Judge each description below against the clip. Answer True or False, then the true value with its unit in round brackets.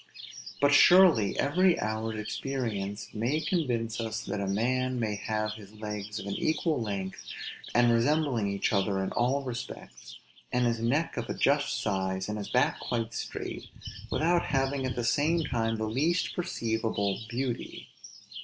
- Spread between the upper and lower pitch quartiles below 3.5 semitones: False (4.4 semitones)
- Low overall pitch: True (115 Hz)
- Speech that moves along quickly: False (155 wpm)